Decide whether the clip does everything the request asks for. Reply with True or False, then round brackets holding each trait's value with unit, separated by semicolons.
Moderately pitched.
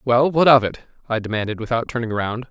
False (120 Hz)